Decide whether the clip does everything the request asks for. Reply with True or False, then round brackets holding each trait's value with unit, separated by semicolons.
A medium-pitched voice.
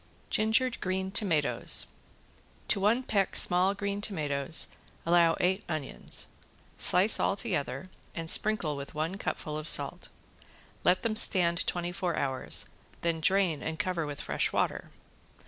True (180 Hz)